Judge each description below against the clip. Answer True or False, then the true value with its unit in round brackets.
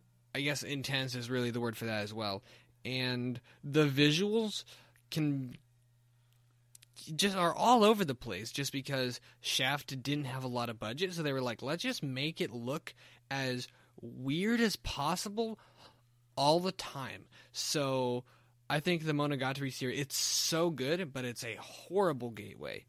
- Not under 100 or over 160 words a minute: True (155 wpm)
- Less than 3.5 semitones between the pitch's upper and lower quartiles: False (4.0 semitones)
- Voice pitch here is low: True (130 Hz)